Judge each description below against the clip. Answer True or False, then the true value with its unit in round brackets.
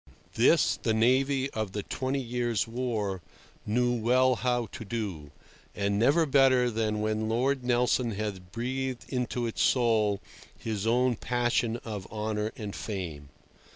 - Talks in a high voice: False (115 Hz)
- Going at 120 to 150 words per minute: True (140 wpm)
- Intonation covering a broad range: False (2.9 semitones)